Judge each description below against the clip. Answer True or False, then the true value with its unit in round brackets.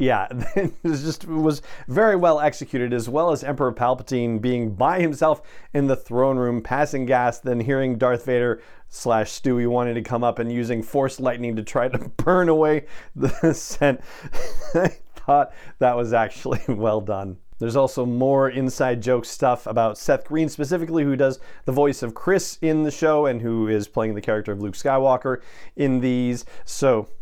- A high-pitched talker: False (130 Hz)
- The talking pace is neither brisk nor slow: True (180 wpm)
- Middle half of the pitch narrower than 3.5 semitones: False (3.8 semitones)